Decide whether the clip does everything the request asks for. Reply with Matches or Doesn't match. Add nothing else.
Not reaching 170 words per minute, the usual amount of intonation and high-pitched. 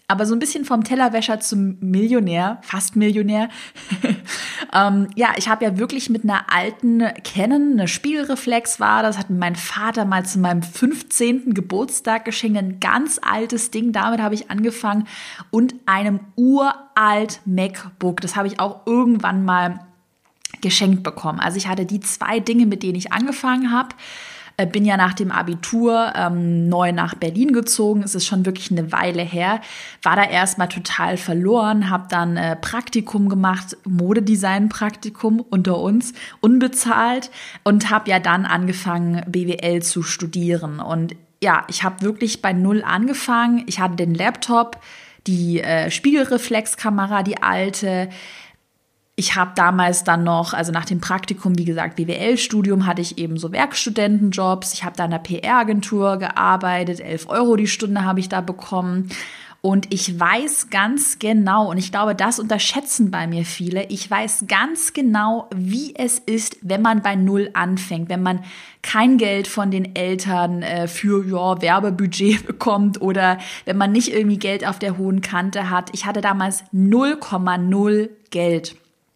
Matches